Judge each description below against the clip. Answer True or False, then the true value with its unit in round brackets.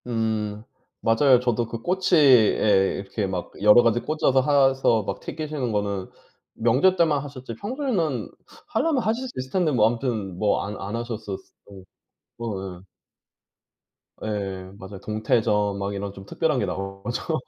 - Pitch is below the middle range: True (115 Hz)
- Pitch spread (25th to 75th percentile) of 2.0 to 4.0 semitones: False (5.3 semitones)